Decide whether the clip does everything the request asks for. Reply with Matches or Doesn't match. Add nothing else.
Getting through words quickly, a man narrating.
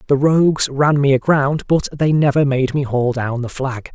Matches